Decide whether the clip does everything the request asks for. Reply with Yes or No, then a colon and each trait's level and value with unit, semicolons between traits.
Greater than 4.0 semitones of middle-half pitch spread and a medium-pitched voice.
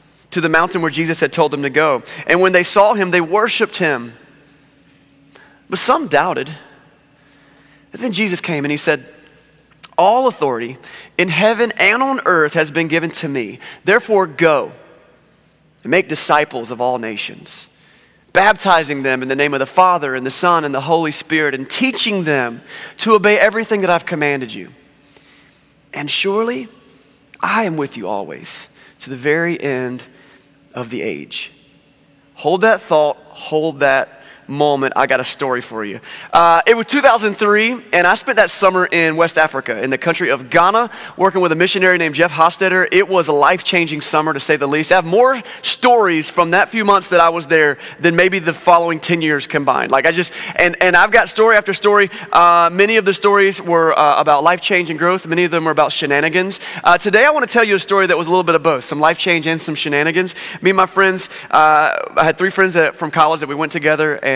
Yes: average, 4.5 semitones; medium, 165 Hz